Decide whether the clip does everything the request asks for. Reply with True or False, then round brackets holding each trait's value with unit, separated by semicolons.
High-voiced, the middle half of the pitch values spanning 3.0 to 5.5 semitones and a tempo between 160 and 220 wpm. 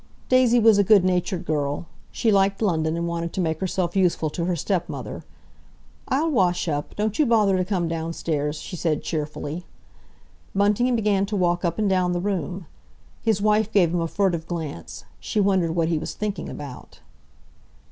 False (180 Hz; 3.6 semitones; 180 wpm)